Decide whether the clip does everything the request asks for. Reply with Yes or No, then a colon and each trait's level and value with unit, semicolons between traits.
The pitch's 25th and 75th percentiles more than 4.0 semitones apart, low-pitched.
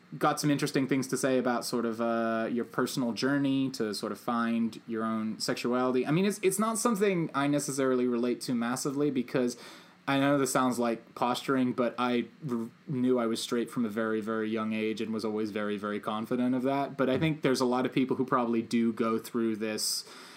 No: average, 3.2 semitones; low, 125 Hz